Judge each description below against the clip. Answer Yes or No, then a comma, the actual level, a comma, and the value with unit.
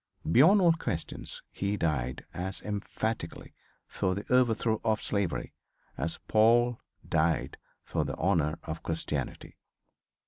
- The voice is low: Yes, low, 100 Hz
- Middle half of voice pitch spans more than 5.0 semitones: Yes, wide, 5.5 semitones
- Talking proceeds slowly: Yes, slow, 115 wpm